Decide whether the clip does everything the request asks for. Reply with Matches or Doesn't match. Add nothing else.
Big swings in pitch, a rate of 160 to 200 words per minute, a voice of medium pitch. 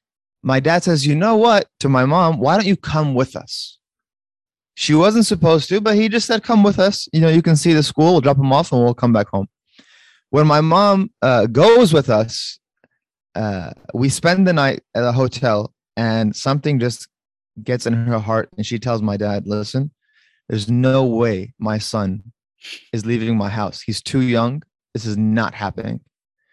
Doesn't match